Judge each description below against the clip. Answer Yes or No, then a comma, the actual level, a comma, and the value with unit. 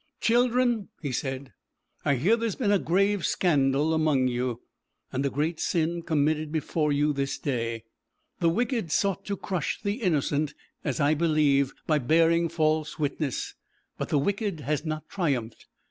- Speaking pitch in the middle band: Yes, medium, 155 Hz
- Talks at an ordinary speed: Yes, average, 160 wpm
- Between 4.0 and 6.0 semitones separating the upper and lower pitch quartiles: Yes, average, 4.4 semitones